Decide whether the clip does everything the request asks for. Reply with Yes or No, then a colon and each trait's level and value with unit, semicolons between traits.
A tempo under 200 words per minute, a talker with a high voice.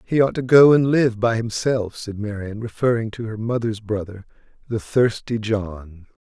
No: average, 175 wpm; low, 110 Hz